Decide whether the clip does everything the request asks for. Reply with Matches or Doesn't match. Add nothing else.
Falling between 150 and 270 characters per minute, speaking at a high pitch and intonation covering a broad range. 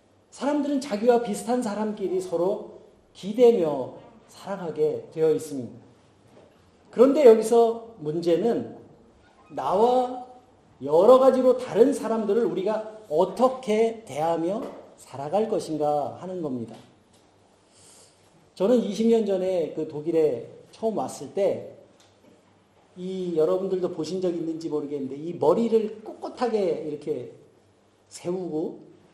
Matches